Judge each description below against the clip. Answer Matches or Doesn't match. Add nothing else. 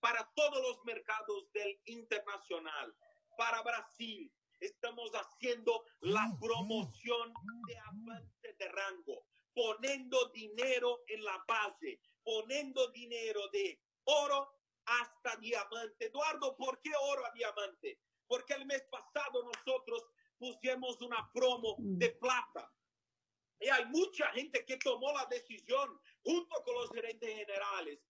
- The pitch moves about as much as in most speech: Matches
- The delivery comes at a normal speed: Doesn't match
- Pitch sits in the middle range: Doesn't match